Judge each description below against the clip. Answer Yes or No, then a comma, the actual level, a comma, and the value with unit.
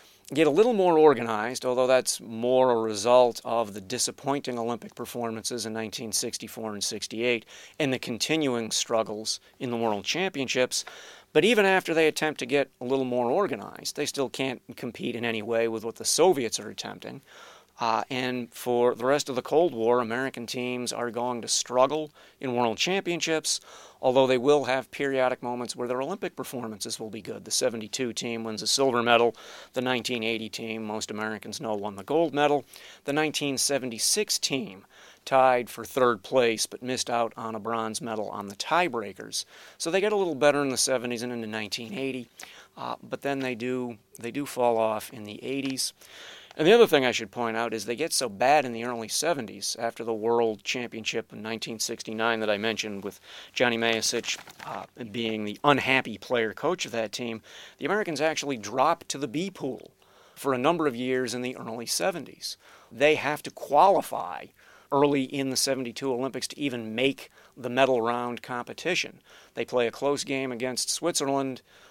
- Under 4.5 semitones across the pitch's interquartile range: Yes, average, 2.9 semitones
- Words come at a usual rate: Yes, average, 180 wpm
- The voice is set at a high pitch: No, low, 125 Hz